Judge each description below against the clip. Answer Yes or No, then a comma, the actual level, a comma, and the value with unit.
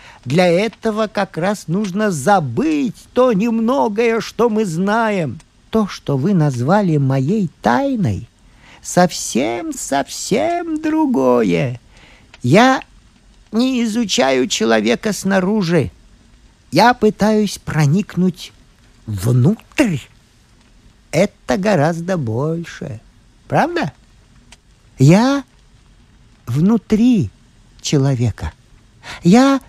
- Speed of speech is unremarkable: No, slow, 75 wpm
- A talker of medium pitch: Yes, medium, 180 Hz